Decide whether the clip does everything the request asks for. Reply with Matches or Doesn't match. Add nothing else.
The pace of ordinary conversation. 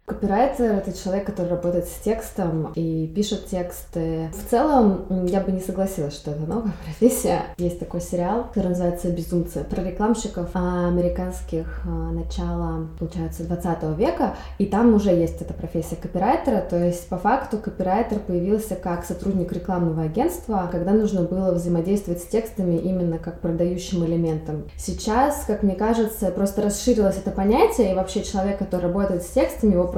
Matches